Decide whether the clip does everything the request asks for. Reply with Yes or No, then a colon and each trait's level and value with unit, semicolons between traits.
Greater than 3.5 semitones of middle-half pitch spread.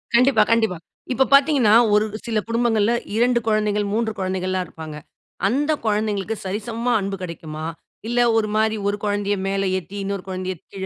No: average, 3.2 semitones